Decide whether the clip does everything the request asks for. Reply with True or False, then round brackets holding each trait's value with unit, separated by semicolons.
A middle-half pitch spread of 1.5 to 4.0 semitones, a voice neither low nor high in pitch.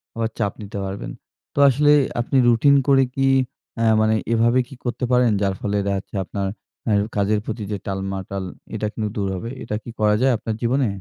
False (3.4 semitones; 110 Hz)